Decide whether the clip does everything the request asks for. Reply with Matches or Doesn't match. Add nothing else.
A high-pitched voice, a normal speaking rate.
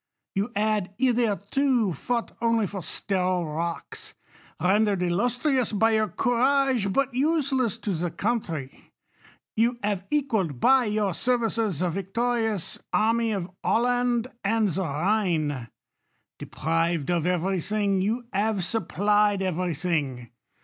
Doesn't match